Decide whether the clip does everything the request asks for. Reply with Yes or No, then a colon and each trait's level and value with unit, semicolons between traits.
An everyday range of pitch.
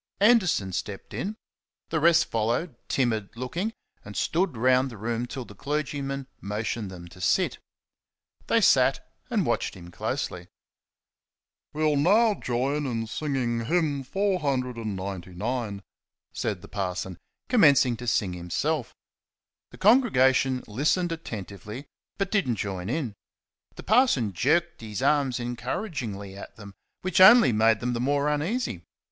No: wide, 6.7 semitones